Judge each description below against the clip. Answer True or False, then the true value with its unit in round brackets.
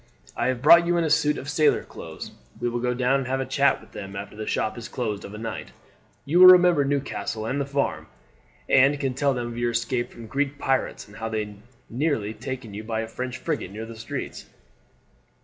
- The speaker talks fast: True (225 wpm)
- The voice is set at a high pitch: False (125 Hz)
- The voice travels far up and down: False (4.0 semitones)